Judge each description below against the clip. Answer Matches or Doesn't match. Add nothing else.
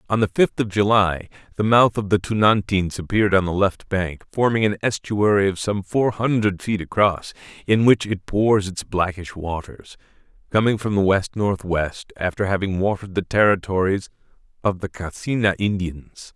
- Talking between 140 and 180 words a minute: Matches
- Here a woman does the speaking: Doesn't match